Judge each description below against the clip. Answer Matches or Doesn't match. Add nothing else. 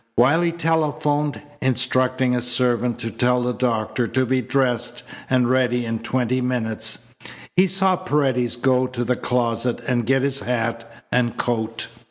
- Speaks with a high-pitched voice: Doesn't match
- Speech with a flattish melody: Matches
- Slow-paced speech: Doesn't match